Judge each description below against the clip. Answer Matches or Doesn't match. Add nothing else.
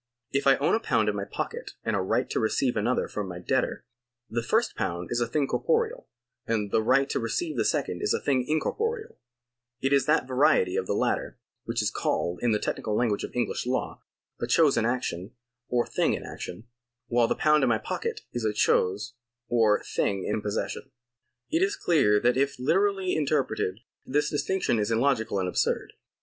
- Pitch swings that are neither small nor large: Doesn't match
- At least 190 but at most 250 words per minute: Matches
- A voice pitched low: Matches